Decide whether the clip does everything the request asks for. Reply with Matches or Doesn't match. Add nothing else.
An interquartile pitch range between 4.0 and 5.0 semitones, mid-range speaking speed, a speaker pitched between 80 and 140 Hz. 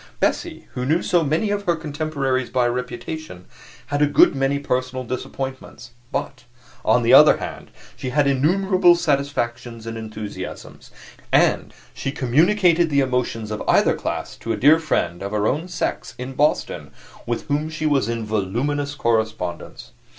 Matches